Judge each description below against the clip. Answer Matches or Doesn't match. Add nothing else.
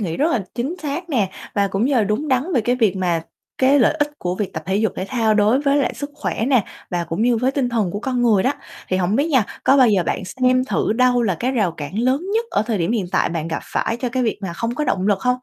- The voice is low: Doesn't match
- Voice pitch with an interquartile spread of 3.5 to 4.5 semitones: Doesn't match